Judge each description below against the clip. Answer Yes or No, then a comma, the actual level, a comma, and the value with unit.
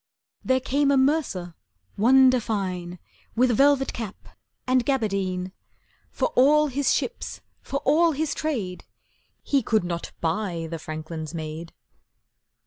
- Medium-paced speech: No, slow, 125 wpm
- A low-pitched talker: No, high, 225 Hz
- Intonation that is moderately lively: No, wide, 7.4 semitones